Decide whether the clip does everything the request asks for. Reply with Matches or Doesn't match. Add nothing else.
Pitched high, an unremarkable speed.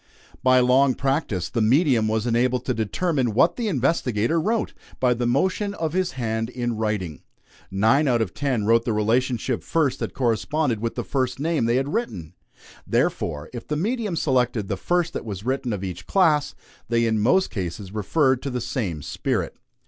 Doesn't match